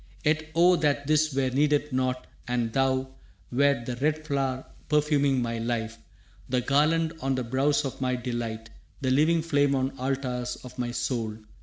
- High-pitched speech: No, low, 130 Hz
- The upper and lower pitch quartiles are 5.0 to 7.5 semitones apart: No, average, 2.9 semitones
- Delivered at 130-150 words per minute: No, average, 165 wpm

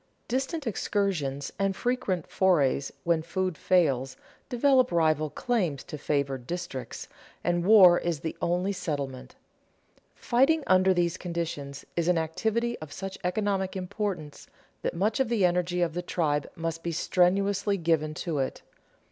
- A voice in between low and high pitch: Yes, medium, 175 Hz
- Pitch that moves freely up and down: No, average, 4.1 semitones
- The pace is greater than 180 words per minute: No, average, 140 wpm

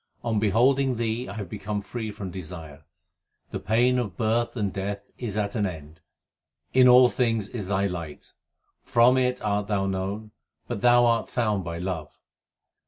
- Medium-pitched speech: No, low, 105 Hz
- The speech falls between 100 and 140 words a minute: No, average, 170 wpm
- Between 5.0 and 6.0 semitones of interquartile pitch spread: No, average, 3.7 semitones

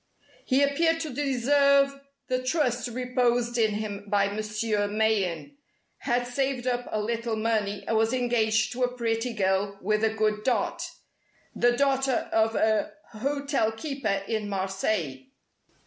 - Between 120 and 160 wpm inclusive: Yes, average, 140 wpm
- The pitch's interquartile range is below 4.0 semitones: Yes, average, 3.1 semitones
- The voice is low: No, high, 230 Hz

